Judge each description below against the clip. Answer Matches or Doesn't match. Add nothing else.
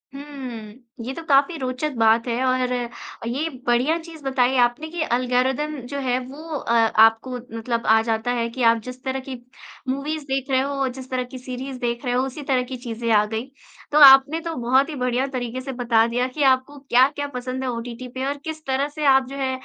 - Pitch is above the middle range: Matches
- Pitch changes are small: Matches